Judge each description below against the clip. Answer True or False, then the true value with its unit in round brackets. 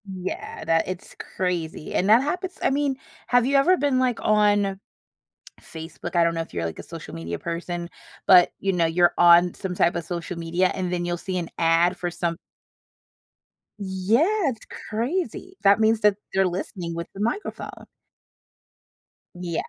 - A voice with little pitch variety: False (4.0 semitones)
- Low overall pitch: False (185 Hz)